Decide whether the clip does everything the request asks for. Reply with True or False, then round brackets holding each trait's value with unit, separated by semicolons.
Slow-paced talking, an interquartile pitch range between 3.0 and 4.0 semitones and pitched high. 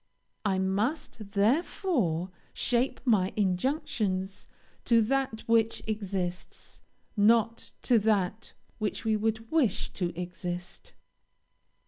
True (95 wpm; 3.4 semitones; 215 Hz)